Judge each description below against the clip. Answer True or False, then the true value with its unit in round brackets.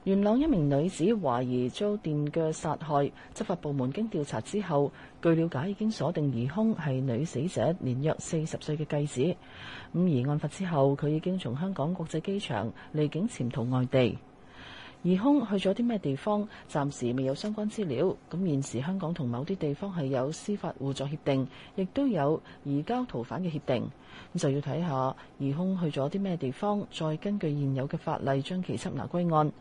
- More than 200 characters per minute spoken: True (275 characters per minute)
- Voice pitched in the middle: True (155 Hz)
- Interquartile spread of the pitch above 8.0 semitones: False (5.4 semitones)